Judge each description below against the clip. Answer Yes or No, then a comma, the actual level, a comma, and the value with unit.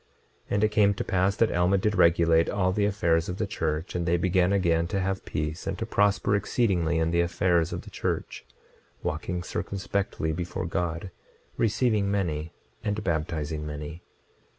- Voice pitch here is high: No, very low, 90 Hz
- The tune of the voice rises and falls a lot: No, average, 3.2 semitones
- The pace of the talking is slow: No, average, 175 wpm